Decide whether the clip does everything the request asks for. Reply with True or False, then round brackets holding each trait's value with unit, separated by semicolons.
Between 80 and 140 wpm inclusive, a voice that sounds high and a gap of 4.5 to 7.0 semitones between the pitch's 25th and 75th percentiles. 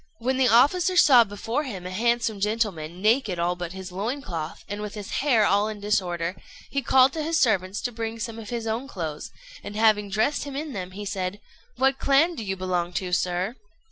False (205 wpm; 215 Hz; 5.0 semitones)